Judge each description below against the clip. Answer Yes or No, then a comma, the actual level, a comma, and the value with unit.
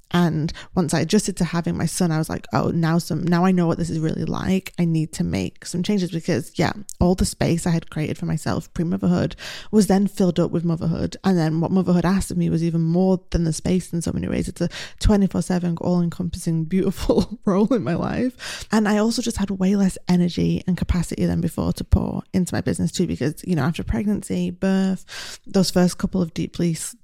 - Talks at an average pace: No, fast, 220 wpm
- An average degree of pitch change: No, narrow, 2.3 semitones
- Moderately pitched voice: Yes, medium, 180 Hz